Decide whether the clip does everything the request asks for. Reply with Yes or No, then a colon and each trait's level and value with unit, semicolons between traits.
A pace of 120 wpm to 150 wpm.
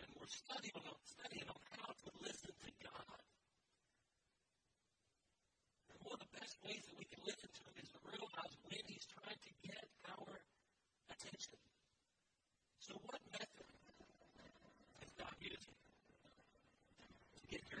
Yes: average, 140 wpm